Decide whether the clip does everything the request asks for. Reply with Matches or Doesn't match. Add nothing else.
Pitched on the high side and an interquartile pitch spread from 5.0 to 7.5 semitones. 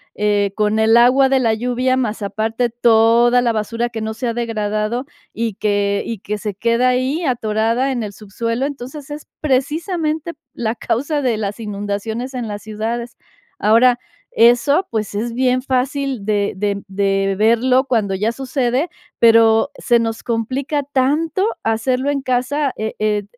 Doesn't match